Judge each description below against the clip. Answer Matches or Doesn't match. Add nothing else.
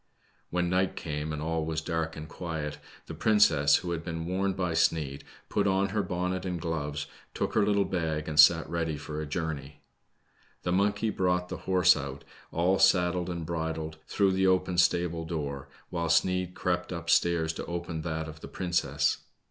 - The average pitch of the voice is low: Matches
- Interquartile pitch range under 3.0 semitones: Matches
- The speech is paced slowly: Doesn't match